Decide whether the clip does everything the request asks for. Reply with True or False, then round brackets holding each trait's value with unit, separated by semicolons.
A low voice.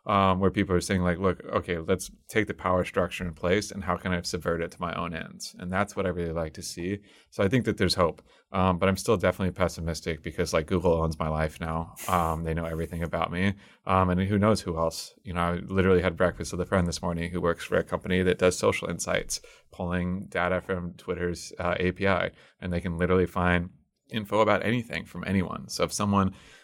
True (90 Hz)